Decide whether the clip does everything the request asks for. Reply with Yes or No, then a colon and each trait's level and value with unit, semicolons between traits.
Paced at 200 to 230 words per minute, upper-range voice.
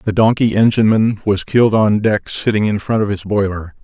No: fast, 205 wpm; low, 105 Hz